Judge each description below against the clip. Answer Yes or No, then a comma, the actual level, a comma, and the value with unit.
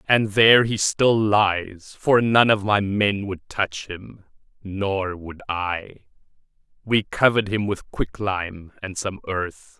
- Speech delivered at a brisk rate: No, average, 145 wpm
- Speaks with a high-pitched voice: No, low, 100 Hz